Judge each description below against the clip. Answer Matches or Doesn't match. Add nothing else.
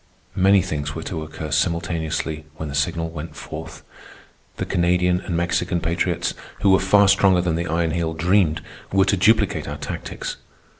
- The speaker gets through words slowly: Doesn't match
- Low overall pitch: Matches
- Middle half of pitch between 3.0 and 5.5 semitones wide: Doesn't match